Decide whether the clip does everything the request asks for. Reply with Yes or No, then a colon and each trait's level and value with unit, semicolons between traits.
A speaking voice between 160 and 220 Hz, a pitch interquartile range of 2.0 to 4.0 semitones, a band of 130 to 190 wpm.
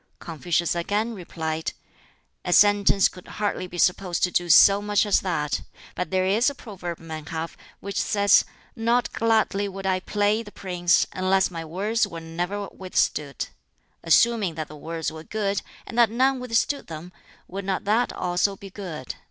Yes: high, 190 Hz; average, 3.4 semitones; average, 170 wpm